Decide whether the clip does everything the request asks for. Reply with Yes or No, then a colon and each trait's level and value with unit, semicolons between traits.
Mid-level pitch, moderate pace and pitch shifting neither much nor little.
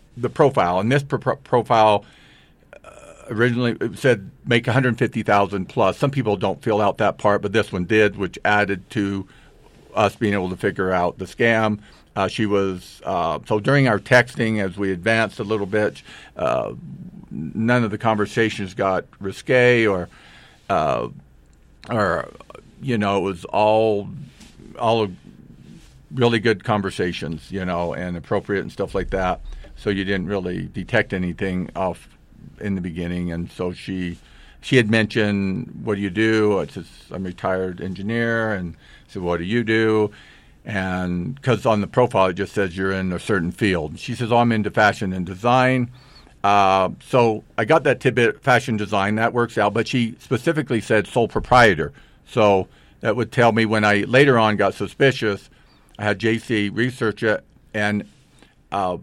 No: low, 105 Hz; average, 170 wpm; average, 3.4 semitones